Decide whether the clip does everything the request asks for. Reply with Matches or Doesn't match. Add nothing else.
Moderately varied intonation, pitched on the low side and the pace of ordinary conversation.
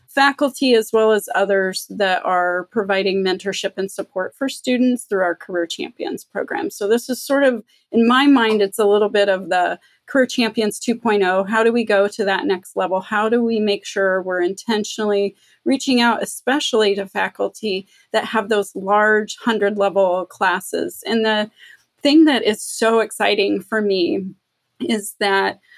Doesn't match